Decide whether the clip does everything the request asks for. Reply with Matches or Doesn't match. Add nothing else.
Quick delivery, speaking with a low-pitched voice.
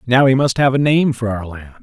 Matches